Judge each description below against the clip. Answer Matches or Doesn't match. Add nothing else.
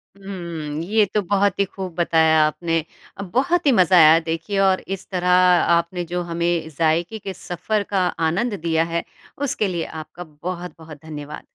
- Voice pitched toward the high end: Doesn't match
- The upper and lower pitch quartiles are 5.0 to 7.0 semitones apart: Doesn't match